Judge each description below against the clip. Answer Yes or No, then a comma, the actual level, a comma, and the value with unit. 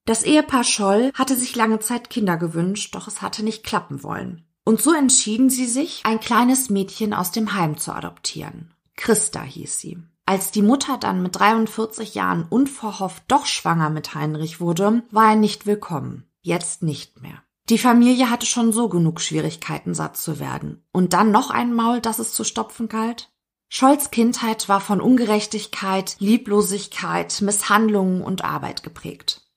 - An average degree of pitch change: Yes, average, 4.6 semitones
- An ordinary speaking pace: Yes, average, 165 wpm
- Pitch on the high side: Yes, high, 210 Hz